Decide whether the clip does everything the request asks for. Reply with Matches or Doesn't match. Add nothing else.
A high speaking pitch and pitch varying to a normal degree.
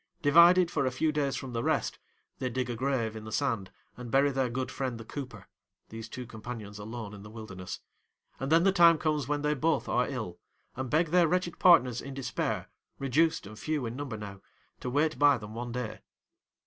Doesn't match